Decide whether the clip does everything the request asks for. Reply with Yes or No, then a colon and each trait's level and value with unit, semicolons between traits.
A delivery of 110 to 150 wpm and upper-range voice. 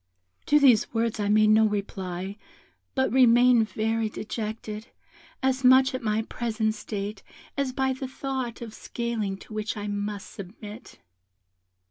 Yes: average, 140 wpm; high, 220 Hz